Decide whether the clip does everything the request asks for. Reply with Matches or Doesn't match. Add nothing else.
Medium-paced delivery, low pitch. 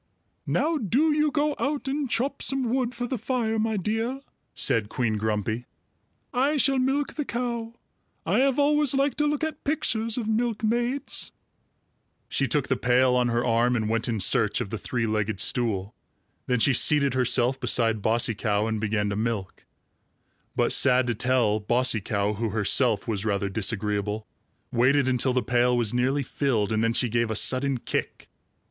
Matches